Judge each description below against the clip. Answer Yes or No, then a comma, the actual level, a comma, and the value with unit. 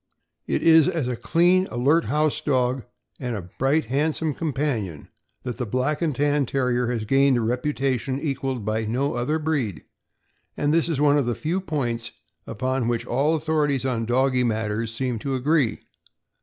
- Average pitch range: Yes, average, 3.7 semitones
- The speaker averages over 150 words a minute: Yes, average, 170 wpm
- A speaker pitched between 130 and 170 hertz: Yes, low, 135 Hz